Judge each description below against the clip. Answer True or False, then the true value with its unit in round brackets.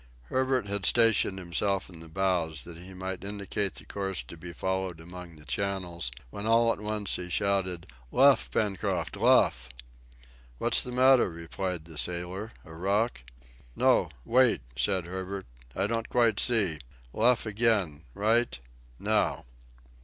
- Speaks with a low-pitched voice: True (95 Hz)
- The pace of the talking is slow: False (145 wpm)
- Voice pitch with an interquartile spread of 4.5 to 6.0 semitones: False (3.9 semitones)